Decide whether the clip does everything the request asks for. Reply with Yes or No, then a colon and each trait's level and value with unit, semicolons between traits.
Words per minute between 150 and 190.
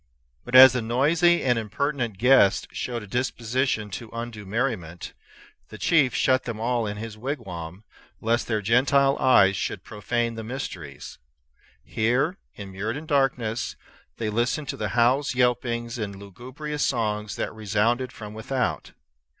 No: average, 140 wpm